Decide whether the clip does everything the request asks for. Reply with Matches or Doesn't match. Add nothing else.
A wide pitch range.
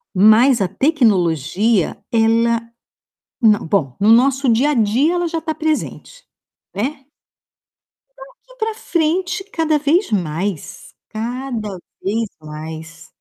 Matches